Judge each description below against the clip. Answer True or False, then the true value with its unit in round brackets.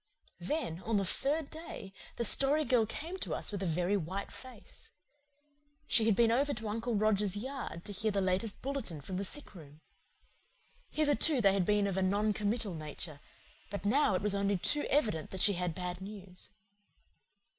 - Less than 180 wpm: False (185 wpm)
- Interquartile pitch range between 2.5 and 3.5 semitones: False (4.5 semitones)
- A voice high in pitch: True (205 Hz)